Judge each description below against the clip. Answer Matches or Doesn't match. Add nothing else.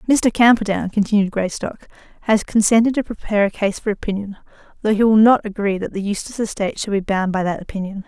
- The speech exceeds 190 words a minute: Matches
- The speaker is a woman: Matches